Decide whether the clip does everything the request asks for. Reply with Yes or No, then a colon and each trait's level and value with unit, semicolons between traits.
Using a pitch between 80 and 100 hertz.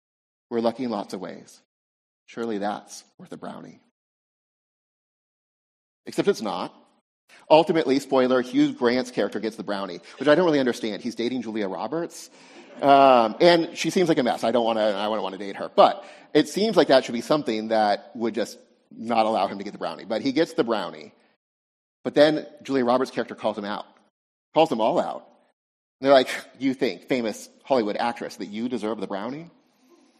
No: low, 120 Hz